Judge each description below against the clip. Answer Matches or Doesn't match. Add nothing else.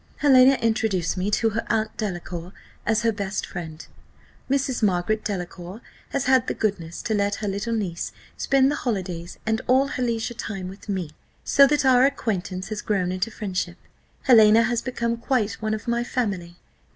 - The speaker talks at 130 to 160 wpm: Doesn't match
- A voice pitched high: Matches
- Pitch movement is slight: Doesn't match